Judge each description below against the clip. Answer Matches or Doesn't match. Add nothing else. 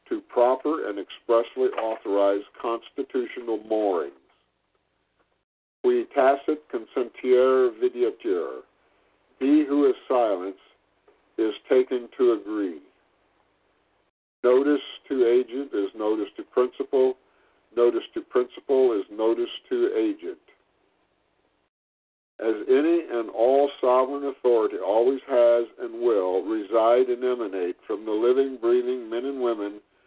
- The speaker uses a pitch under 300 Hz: Doesn't match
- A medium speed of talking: Doesn't match